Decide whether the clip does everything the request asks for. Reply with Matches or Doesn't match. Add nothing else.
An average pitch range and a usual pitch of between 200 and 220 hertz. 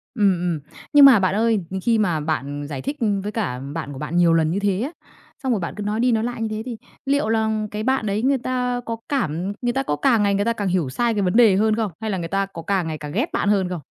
Matches